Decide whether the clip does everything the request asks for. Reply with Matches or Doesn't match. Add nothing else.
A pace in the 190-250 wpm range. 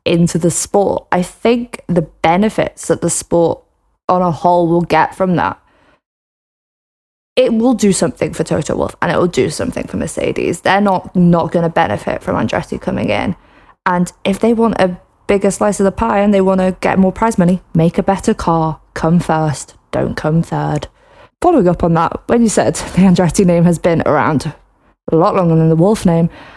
Matches